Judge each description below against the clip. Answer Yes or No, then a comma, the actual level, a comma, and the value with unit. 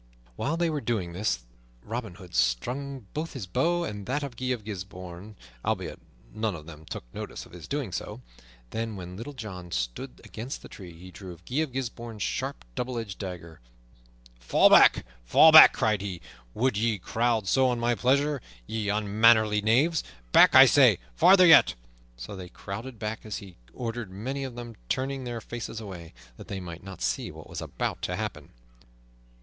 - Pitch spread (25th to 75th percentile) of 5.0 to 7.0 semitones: Yes, wide, 5.5 semitones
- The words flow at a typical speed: Yes, average, 180 wpm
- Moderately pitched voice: No, low, 110 Hz